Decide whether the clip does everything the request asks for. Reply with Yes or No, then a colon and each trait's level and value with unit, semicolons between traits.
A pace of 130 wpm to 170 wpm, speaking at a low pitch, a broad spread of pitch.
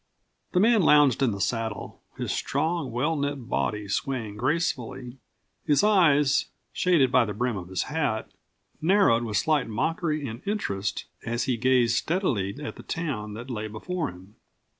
Yes: average, 160 wpm; low, 130 Hz; wide, 6.2 semitones